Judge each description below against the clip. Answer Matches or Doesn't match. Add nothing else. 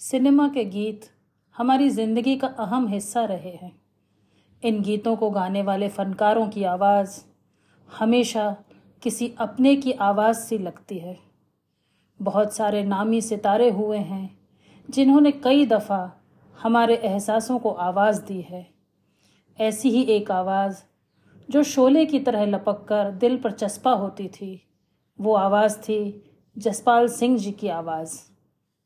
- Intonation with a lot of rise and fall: Doesn't match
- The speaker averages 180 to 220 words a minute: Doesn't match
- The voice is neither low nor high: Doesn't match